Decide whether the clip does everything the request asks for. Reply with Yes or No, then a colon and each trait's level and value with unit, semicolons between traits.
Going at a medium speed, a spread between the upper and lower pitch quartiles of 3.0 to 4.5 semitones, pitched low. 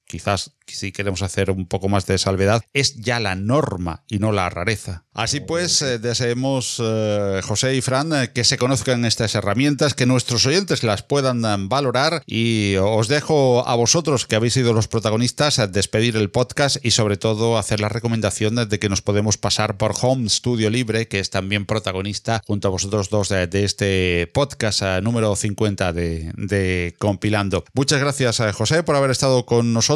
Yes: average, 175 wpm; average, 3.9 semitones; low, 110 Hz